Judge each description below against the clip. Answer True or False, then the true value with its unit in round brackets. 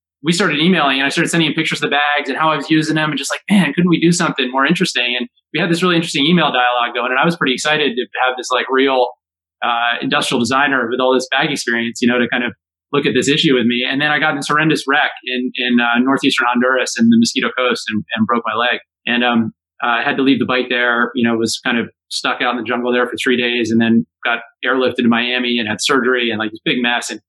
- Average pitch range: True (3.8 semitones)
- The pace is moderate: False (275 wpm)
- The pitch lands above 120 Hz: True (130 Hz)